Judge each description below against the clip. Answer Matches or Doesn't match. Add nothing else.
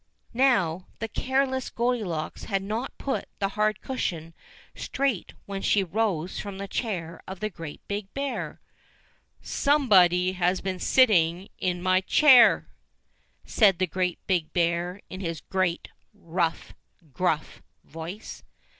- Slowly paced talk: Matches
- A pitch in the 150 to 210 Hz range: Matches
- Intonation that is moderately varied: Matches